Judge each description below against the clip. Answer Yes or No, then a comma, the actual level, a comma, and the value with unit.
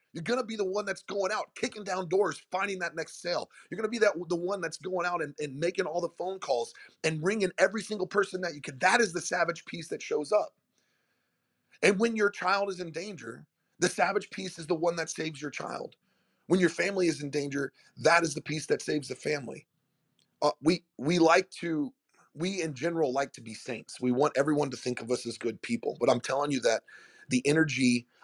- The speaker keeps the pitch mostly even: No, average, 4.2 semitones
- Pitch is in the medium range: Yes, medium, 170 Hz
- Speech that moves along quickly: Yes, fast, 225 wpm